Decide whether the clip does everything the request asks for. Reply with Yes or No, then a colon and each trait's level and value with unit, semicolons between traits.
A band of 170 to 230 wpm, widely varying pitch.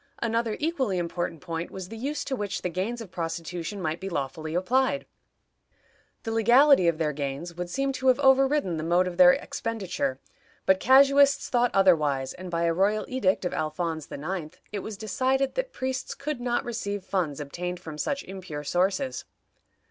Yes: average, 175 wpm; wide, 6.6 semitones